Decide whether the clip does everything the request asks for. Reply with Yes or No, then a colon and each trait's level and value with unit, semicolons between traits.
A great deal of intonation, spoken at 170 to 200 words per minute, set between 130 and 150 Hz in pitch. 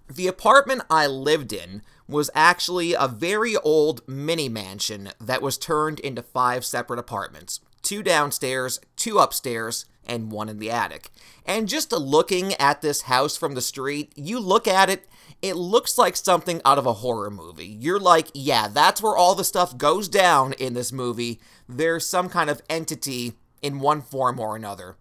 Yes: wide, 5.7 semitones; average, 175 wpm; medium, 140 Hz